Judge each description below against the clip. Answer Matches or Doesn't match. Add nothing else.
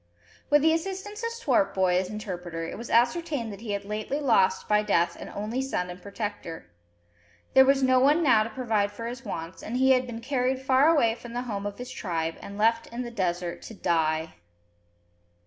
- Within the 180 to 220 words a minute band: Matches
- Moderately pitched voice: Doesn't match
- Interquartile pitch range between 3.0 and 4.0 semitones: Doesn't match